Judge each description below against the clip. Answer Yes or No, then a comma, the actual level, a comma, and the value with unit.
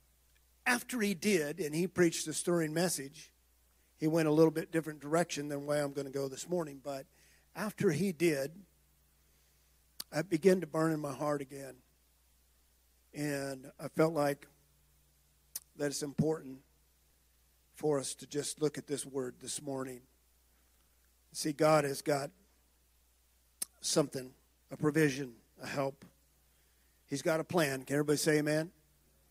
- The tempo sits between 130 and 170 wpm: Yes, average, 145 wpm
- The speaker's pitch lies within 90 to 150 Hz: Yes, medium, 140 Hz